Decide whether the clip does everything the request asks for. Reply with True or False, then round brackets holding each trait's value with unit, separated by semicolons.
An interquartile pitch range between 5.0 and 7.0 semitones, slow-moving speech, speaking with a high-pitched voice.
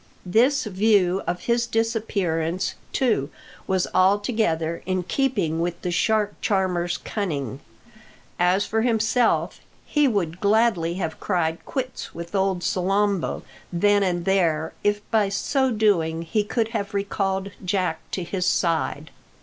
False (4.0 semitones; 130 wpm; 195 Hz)